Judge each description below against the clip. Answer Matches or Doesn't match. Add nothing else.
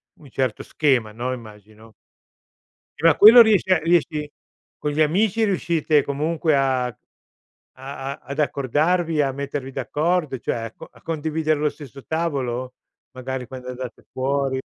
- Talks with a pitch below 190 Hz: Matches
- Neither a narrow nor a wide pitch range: Matches